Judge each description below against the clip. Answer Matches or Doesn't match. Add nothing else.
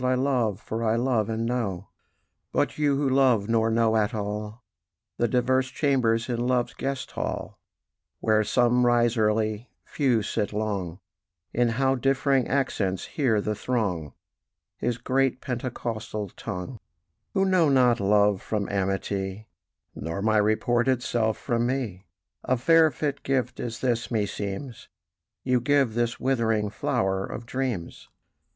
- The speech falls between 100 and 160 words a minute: Matches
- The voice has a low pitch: Matches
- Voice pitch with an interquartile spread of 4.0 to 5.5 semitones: Doesn't match